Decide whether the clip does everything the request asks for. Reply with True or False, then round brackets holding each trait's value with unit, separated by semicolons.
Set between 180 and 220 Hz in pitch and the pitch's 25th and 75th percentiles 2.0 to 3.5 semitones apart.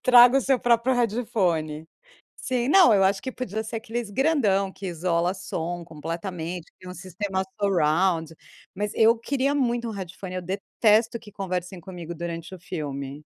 False (190 Hz; 5.2 semitones)